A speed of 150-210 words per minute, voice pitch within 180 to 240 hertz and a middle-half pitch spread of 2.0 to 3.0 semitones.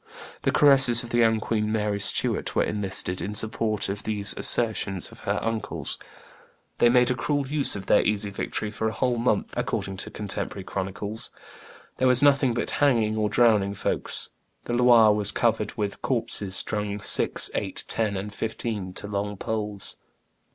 No: average, 170 wpm; low, 110 Hz; average, 2.7 semitones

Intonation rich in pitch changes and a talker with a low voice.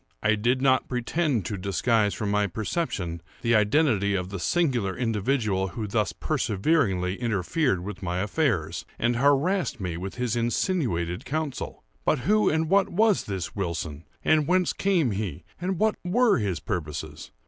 Yes: wide, 8.2 semitones; low, 110 Hz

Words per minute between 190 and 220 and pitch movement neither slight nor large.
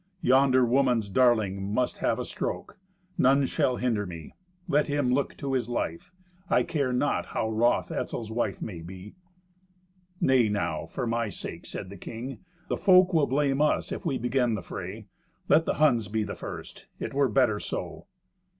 No: average, 175 wpm; average, 4.4 semitones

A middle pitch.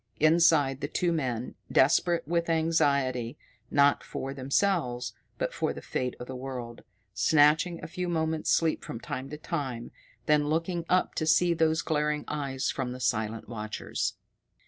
Yes: medium, 150 Hz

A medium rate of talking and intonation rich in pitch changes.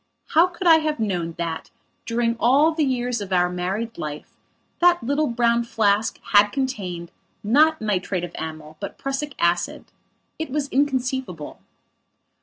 Yes: average, 145 wpm; wide, 7.5 semitones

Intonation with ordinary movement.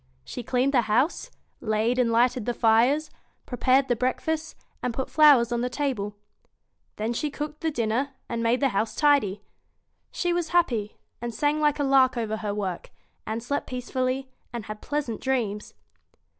Yes: average, 3.9 semitones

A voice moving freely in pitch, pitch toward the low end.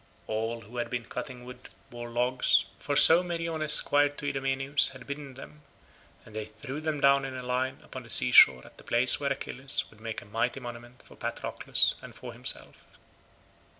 No: average, 3.0 semitones; low, 130 Hz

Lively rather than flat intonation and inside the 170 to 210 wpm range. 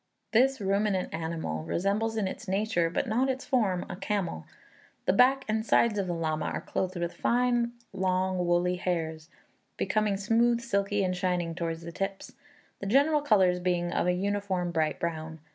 No: average, 3.9 semitones; average, 175 wpm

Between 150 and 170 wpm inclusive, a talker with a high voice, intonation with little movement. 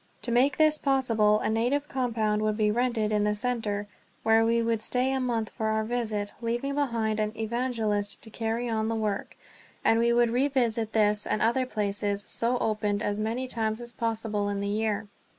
No: average, 195 wpm; high, 225 Hz; narrow, 2.3 semitones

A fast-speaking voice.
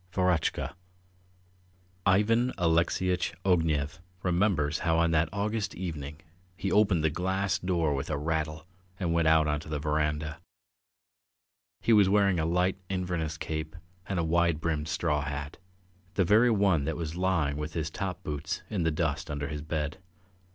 No: average, 160 wpm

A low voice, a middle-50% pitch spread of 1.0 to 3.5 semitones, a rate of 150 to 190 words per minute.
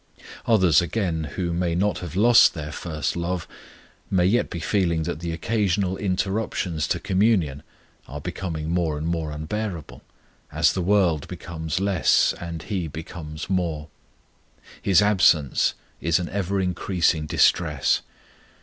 No: very low, 85 Hz; average, 3.2 semitones; slow, 135 wpm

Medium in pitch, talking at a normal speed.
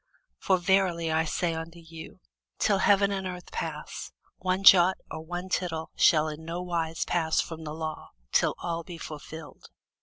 Yes: medium, 170 Hz; average, 170 wpm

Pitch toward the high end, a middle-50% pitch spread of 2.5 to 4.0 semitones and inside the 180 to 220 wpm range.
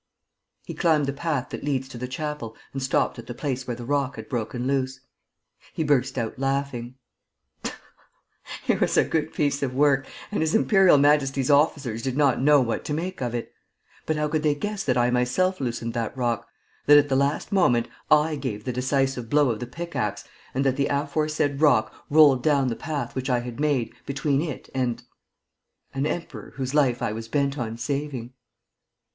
No: low, 135 Hz; average, 3.1 semitones; average, 195 wpm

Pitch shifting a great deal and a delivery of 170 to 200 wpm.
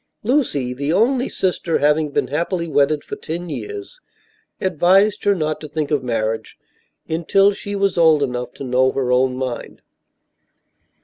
No: wide, 6.7 semitones; average, 150 wpm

